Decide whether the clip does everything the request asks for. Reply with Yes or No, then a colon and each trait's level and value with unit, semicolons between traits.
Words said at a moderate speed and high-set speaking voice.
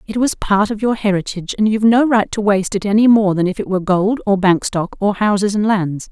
No: fast, 265 wpm; high, 205 Hz